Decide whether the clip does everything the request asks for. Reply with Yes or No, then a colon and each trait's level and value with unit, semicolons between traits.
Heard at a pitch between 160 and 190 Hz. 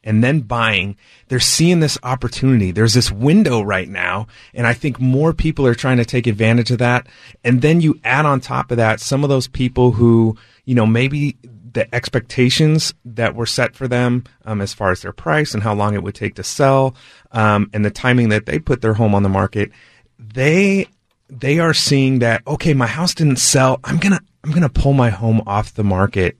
No: low, 125 Hz